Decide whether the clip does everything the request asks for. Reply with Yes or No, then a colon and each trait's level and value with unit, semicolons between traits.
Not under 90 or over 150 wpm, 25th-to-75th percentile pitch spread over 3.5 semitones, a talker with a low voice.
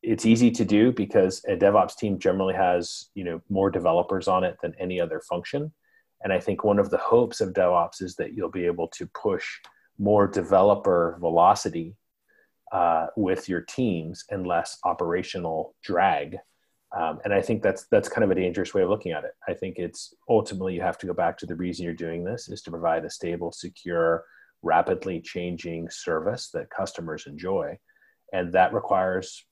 No: average, 185 wpm; average, 4.6 semitones; very low, 95 Hz